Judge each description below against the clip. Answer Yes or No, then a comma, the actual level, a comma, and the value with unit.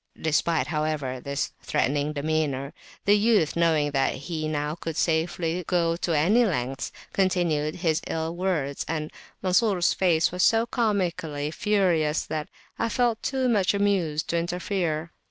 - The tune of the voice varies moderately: Yes, average, 3.6 semitones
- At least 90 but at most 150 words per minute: Yes, average, 140 wpm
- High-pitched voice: No, medium, 165 Hz